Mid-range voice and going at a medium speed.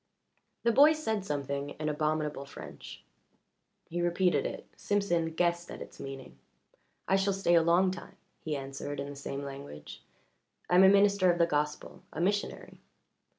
Yes: medium, 170 Hz; average, 160 wpm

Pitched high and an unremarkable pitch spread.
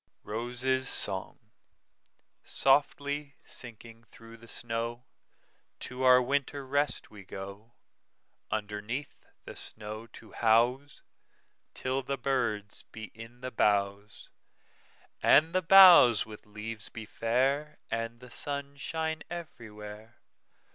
No: low, 120 Hz; average, 4.1 semitones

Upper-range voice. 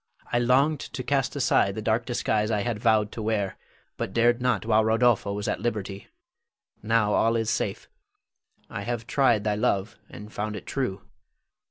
No: low, 110 Hz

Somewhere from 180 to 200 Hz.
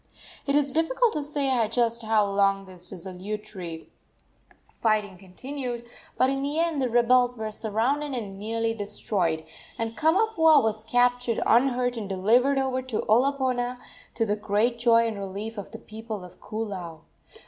No: high, 230 Hz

